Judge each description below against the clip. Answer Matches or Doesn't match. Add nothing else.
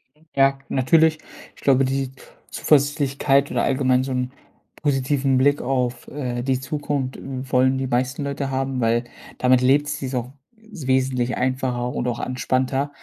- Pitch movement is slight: Matches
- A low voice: Matches